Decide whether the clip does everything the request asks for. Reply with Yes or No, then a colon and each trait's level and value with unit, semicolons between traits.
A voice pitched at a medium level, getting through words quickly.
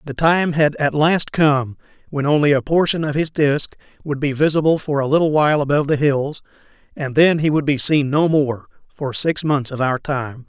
Yes: medium, 145 Hz; fast, 210 wpm